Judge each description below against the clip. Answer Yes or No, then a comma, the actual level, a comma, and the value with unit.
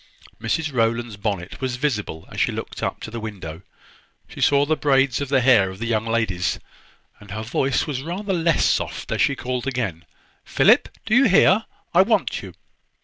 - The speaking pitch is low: Yes, low, 125 Hz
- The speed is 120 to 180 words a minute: No, average, 190 wpm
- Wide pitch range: No, average, 5.0 semitones